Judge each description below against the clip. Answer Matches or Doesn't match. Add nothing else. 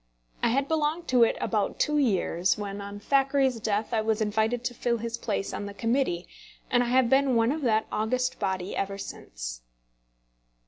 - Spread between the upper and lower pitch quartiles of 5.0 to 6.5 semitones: Doesn't match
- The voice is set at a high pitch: Matches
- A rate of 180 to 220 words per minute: Matches